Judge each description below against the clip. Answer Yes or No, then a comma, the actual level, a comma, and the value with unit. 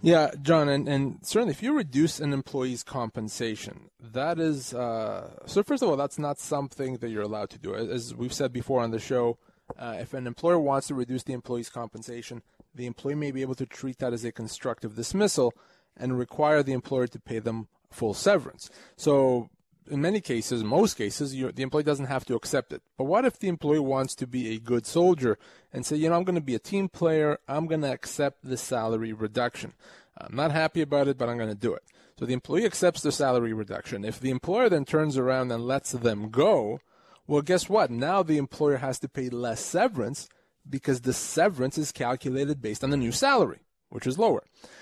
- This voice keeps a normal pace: No, fast, 210 wpm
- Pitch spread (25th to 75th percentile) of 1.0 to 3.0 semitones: No, average, 3.9 semitones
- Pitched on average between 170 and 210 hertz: No, low, 135 Hz